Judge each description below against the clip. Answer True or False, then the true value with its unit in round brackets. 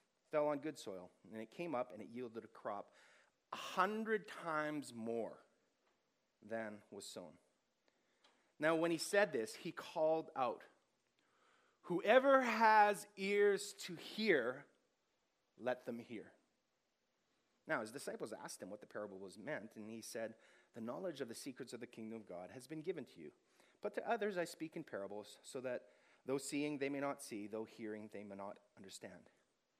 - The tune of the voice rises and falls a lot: True (7.5 semitones)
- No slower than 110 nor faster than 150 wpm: False (170 wpm)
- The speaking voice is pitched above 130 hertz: True (140 Hz)